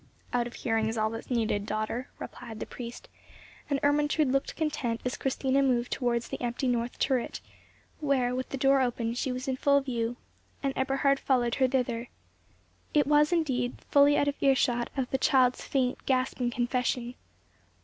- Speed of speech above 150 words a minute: Yes, average, 175 wpm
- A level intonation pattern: Yes, narrow, 2.3 semitones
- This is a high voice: Yes, very high, 255 Hz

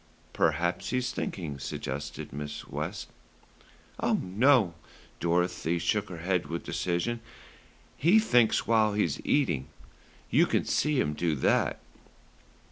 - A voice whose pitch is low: Yes, very low, 90 Hz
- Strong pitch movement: Yes, wide, 6.3 semitones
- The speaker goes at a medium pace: No, slow, 120 wpm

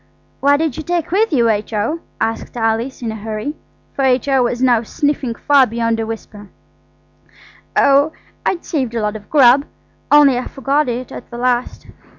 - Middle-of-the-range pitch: No, very high, 250 Hz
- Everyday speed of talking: Yes, average, 170 wpm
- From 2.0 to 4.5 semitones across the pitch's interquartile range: Yes, average, 4.0 semitones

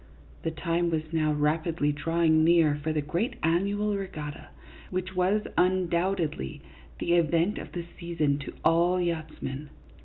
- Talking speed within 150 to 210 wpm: No, slow, 135 wpm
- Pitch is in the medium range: Yes, medium, 165 Hz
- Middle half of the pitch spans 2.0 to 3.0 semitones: Yes, narrow, 2.6 semitones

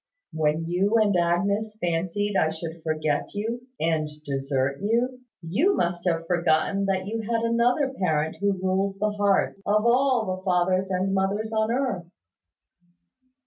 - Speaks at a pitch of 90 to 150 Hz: No, high, 195 Hz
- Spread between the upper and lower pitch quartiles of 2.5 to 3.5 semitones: No, average, 4.4 semitones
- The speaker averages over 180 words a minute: No, average, 145 wpm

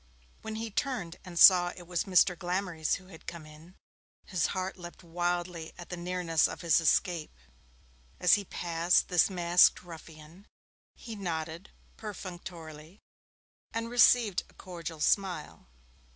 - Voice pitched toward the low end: No, medium, 175 Hz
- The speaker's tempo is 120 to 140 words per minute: Yes, slow, 135 wpm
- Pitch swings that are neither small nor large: No, narrow, 2.2 semitones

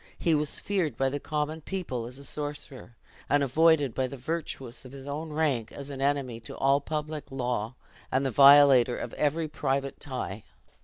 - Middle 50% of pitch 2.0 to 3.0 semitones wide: Yes, narrow, 2.6 semitones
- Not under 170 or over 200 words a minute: Yes, average, 185 wpm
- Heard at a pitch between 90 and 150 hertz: Yes, medium, 140 Hz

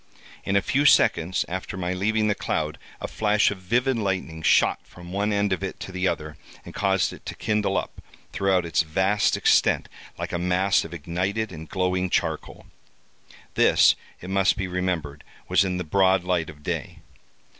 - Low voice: Yes, very low, 95 Hz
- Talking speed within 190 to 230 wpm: No, average, 180 wpm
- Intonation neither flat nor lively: No, narrow, 2.1 semitones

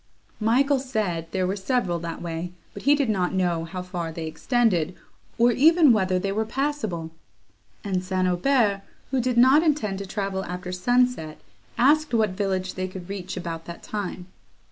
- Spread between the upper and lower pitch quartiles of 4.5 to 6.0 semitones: Yes, average, 5.3 semitones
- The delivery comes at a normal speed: Yes, average, 170 wpm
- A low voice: No, high, 195 Hz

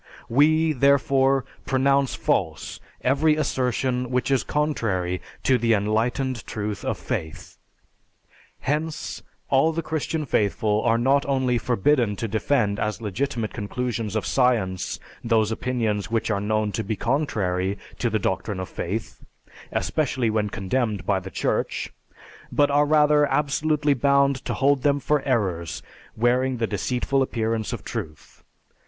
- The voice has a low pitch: Yes, low, 125 Hz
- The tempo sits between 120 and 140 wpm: Yes, slow, 135 wpm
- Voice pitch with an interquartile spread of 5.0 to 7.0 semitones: No, average, 4.5 semitones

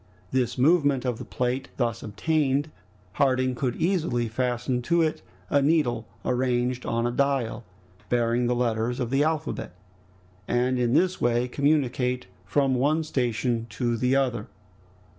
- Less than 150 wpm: Yes, average, 140 wpm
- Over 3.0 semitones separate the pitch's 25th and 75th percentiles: No, average, 2.7 semitones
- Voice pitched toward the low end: Yes, low, 125 Hz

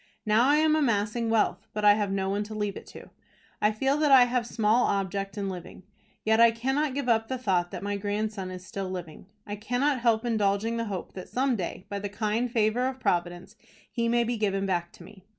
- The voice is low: No, high, 215 Hz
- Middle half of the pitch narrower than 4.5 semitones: Yes, average, 3.3 semitones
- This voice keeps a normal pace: No, fast, 225 wpm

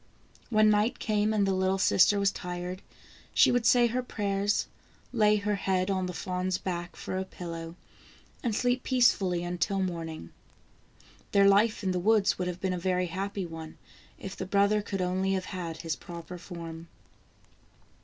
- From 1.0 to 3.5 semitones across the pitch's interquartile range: Yes, narrow, 2.6 semitones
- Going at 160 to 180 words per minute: Yes, average, 170 wpm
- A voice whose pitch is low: No, high, 190 Hz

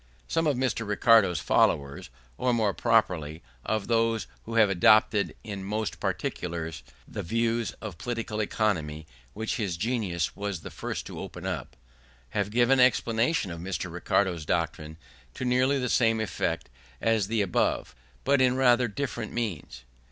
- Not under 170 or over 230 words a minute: No, average, 150 wpm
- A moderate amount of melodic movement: Yes, average, 5.0 semitones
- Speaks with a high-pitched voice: No, low, 110 Hz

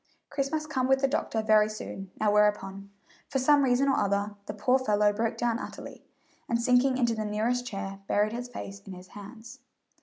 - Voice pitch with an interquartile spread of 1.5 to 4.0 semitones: Yes, average, 3.5 semitones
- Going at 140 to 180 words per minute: No, average, 195 wpm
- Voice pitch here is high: Yes, high, 225 Hz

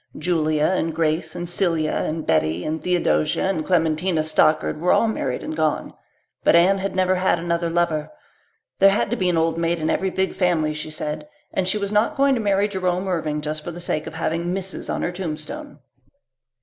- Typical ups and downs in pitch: Yes, average, 3.3 semitones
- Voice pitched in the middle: Yes, medium, 170 Hz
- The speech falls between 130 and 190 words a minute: No, average, 200 wpm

